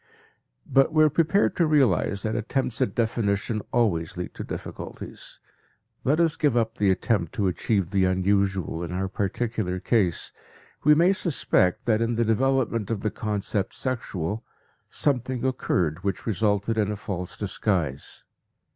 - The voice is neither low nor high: No, low, 110 Hz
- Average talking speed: Yes, average, 150 wpm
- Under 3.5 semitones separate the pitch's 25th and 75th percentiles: No, average, 4.7 semitones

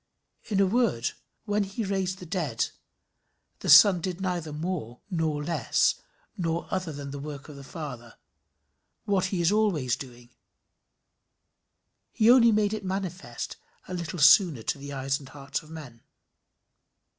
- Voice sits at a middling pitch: Yes, medium, 165 Hz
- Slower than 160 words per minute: Yes, average, 150 wpm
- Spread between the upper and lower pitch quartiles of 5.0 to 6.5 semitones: Yes, average, 5.3 semitones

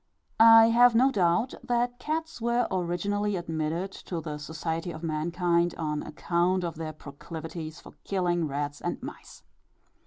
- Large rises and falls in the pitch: Yes, wide, 5.8 semitones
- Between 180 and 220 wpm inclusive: No, average, 145 wpm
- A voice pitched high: No, medium, 175 Hz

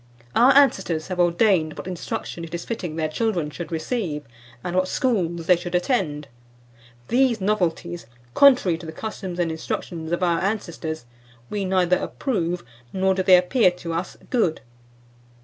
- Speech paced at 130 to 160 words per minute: Yes, average, 155 wpm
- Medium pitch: Yes, medium, 180 Hz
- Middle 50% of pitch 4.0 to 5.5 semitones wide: No, average, 3.2 semitones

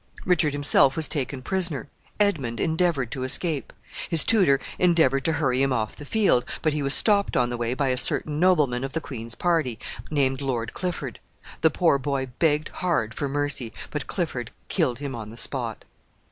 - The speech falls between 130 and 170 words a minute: No, average, 185 wpm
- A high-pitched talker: No, medium, 140 Hz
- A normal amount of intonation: Yes, average, 4.1 semitones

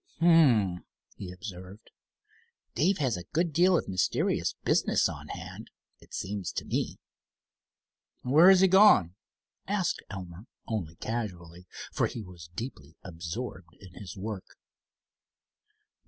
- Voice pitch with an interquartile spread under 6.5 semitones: No, wide, 8.7 semitones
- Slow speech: Yes, slow, 125 wpm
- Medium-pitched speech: No, low, 100 Hz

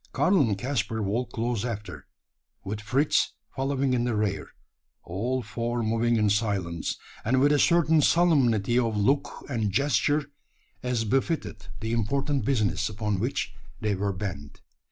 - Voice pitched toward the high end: No, low, 115 Hz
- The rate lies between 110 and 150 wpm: Yes, average, 145 wpm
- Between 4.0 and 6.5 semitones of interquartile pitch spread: Yes, average, 4.4 semitones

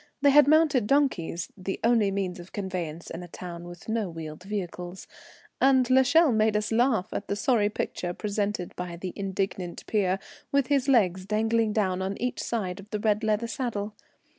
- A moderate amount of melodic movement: Yes, average, 4.2 semitones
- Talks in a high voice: Yes, high, 205 Hz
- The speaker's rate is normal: Yes, average, 180 wpm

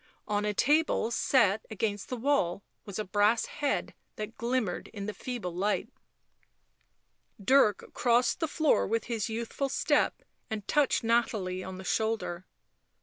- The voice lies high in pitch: Yes, high, 220 Hz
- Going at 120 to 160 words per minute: Yes, average, 145 wpm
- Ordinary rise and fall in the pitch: Yes, average, 3.5 semitones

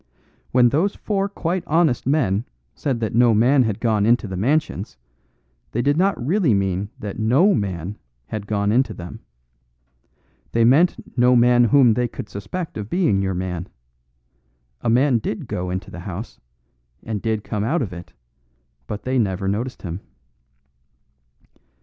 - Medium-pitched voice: No, low, 115 Hz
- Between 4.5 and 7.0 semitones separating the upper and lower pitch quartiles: Yes, average, 5.1 semitones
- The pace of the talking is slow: No, average, 155 wpm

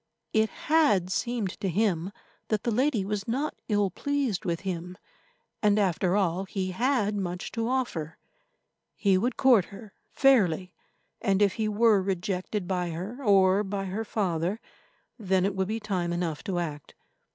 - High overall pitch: Yes, high, 195 Hz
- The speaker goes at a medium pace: Yes, average, 160 wpm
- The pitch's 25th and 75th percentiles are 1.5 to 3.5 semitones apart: Yes, average, 3.2 semitones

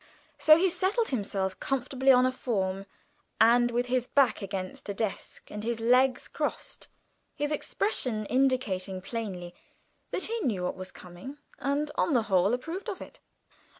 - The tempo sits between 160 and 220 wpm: No, average, 150 wpm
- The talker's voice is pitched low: No, high, 245 Hz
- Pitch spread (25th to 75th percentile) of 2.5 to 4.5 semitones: No, wide, 5.6 semitones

